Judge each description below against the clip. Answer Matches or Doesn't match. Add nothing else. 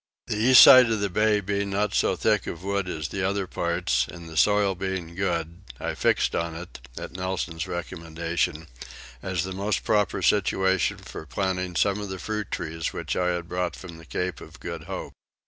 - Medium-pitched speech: Doesn't match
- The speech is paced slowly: Doesn't match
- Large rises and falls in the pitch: Doesn't match